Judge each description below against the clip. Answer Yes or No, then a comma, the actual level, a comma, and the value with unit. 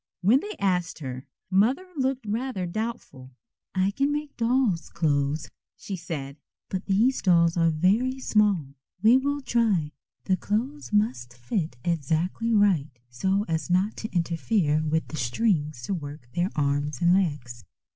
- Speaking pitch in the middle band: Yes, medium, 180 Hz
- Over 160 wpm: No, average, 145 wpm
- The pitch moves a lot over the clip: Yes, wide, 6.6 semitones